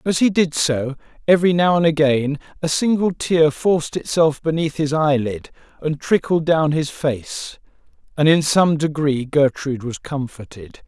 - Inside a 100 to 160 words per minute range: Yes, average, 155 wpm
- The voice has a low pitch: No, medium, 150 Hz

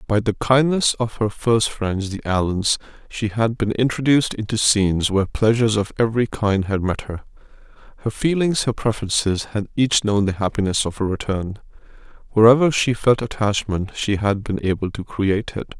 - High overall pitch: No, low, 110 Hz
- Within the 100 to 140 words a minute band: No, average, 175 wpm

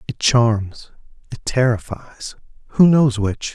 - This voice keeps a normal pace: No, slow, 120 wpm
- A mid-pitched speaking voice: No, low, 120 Hz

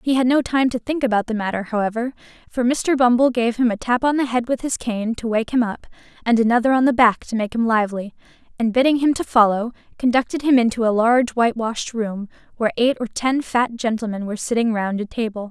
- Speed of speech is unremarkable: No, fast, 230 wpm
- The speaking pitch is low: No, high, 235 Hz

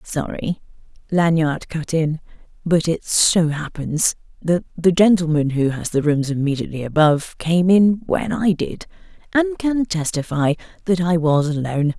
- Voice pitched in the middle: Yes, medium, 165 Hz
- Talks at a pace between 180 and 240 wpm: No, average, 145 wpm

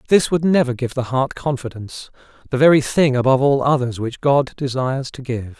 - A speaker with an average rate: Yes, average, 180 wpm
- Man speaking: Yes, male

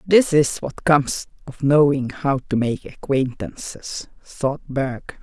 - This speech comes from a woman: Yes, female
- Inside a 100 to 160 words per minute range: Yes, average, 140 wpm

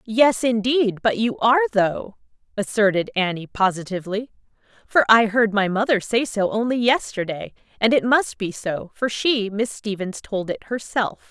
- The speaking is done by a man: No, female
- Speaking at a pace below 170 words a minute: Yes, average, 160 wpm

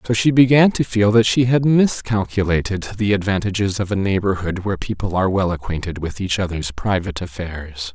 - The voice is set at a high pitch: No, low, 100 Hz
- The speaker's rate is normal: Yes, average, 180 wpm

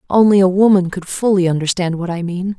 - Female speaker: Yes, female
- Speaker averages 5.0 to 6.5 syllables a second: Yes, 5.9 syllables/s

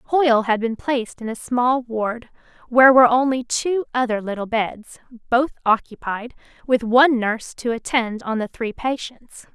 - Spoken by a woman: Yes, female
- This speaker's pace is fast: No, average, 165 wpm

